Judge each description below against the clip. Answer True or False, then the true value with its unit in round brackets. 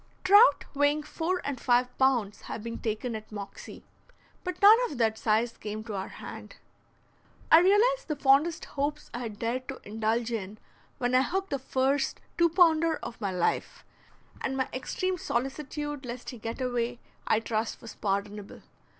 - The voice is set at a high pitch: True (255 Hz)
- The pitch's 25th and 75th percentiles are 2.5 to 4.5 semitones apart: False (5.2 semitones)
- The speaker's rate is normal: True (165 wpm)